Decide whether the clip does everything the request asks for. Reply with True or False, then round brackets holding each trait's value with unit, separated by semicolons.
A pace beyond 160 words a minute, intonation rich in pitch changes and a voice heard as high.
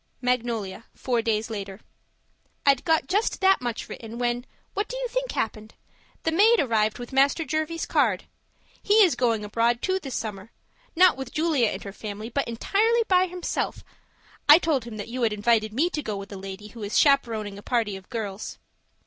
True (190 wpm; 6.9 semitones; 240 Hz)